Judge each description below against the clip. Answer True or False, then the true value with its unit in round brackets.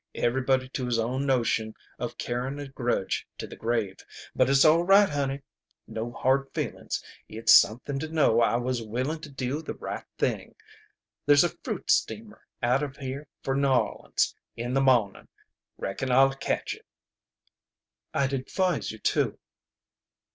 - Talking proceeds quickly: False (155 wpm)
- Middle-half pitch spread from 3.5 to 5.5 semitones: False (2.7 semitones)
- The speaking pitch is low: True (130 Hz)